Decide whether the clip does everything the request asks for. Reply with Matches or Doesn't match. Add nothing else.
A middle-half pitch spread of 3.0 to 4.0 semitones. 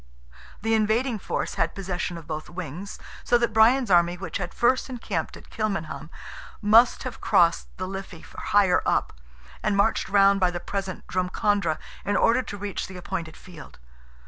Matches